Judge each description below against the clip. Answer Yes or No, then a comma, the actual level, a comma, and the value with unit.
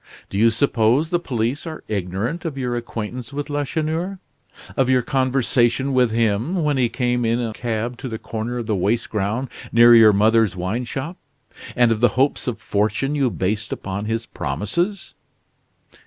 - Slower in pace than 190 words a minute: Yes, average, 170 wpm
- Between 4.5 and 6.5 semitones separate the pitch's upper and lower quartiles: No, average, 3.6 semitones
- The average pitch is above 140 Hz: No, low, 120 Hz